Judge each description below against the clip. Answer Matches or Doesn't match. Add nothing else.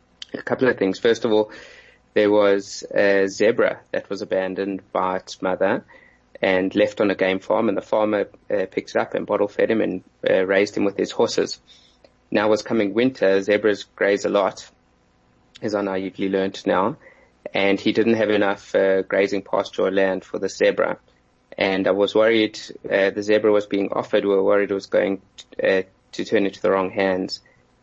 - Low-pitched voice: Matches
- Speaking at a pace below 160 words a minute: Doesn't match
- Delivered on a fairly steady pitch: Matches